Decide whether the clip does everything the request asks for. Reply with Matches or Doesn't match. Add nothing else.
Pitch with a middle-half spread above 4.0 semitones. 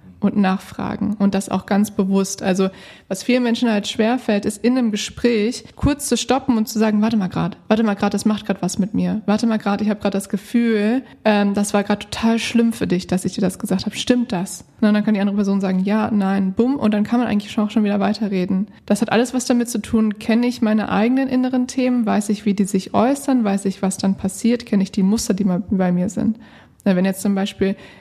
Doesn't match